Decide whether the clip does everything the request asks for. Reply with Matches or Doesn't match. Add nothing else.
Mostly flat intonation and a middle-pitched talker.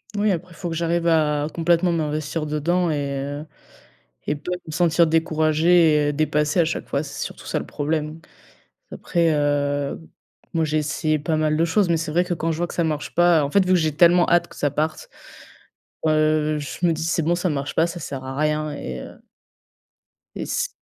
Matches